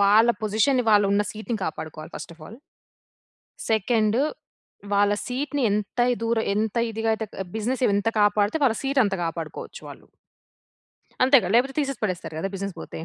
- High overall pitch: Yes, high, 215 Hz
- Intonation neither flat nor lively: Yes, average, 3.2 semitones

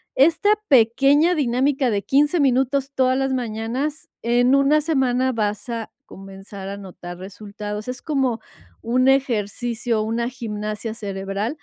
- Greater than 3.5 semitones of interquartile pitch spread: Yes, average, 4.2 semitones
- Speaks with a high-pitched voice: Yes, high, 240 Hz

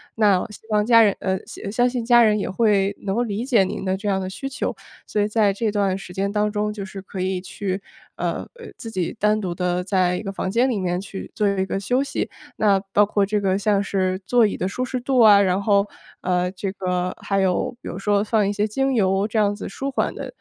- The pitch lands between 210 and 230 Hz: No, high, 200 Hz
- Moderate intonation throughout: No, narrow, 2.3 semitones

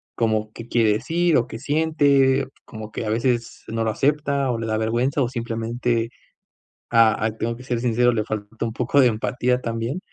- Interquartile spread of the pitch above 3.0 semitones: No, average, 2.7 semitones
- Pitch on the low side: Yes, low, 115 Hz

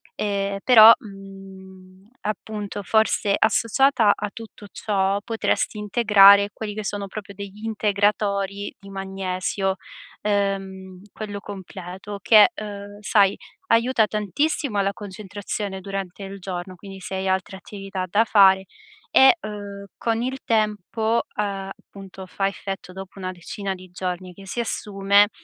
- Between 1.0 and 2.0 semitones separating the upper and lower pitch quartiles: Yes, narrow, 1.7 semitones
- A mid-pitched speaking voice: No, high, 200 Hz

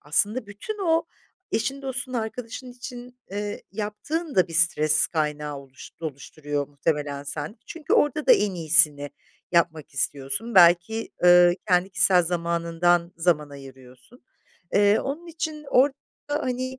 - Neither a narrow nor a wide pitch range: No, wide, 8.4 semitones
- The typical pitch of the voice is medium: Yes, medium, 180 Hz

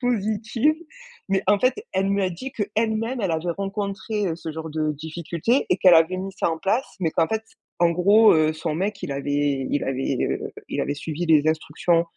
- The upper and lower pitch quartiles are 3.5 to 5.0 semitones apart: Yes, average, 4.7 semitones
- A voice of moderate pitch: Yes, medium, 180 Hz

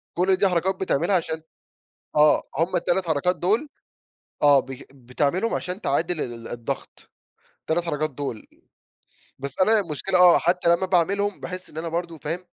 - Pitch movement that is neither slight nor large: Yes, average, 3.7 semitones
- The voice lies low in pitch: No, medium, 170 Hz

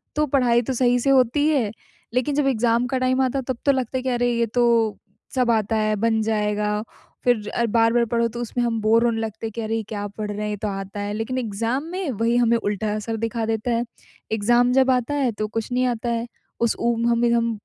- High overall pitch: Yes, high, 235 Hz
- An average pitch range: No, narrow, 2.3 semitones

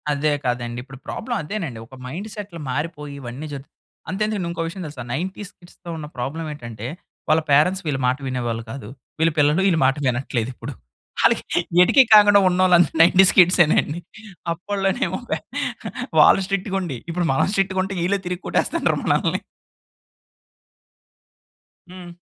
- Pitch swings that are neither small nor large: No, wide, 5.7 semitones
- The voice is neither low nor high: Yes, medium, 165 Hz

